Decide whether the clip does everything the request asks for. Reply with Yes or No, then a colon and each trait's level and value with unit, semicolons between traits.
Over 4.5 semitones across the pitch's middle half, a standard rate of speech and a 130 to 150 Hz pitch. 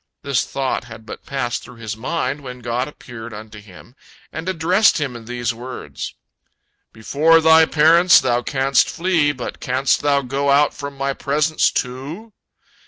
No: average, 3.9 semitones; average, 160 wpm; low, 135 Hz